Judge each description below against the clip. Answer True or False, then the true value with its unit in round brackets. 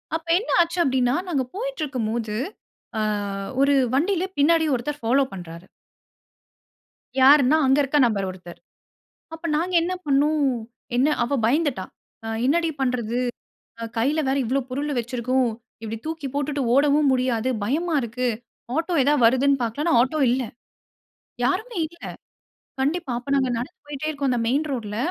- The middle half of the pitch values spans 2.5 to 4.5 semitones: True (4.1 semitones)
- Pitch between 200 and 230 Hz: False (275 Hz)